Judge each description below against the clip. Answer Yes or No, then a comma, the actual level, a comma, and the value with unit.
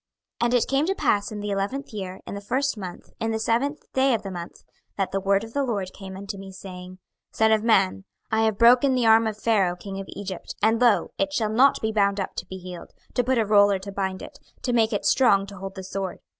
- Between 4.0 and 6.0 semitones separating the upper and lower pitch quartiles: No, average, 3.1 semitones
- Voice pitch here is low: No, high, 205 Hz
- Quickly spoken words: Yes, fast, 260 wpm